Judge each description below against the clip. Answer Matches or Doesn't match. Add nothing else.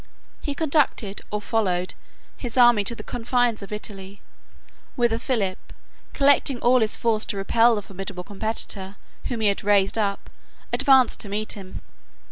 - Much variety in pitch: Doesn't match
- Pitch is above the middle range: Matches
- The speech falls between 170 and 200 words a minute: Doesn't match